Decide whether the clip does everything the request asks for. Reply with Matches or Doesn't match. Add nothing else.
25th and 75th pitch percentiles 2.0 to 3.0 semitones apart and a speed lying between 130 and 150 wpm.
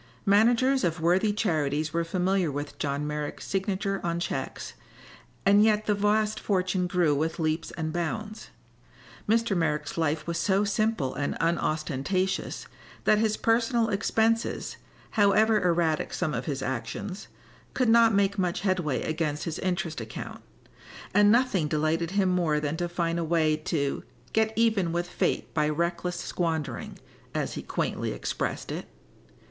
Doesn't match